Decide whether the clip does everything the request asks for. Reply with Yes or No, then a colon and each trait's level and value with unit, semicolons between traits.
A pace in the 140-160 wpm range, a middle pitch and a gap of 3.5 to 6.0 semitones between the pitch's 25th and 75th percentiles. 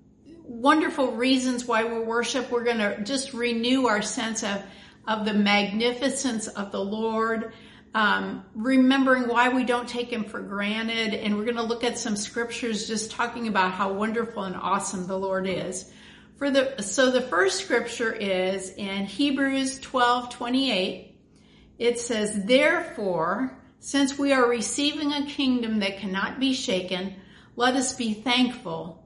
No: average, 155 wpm; high, 235 Hz; average, 3.8 semitones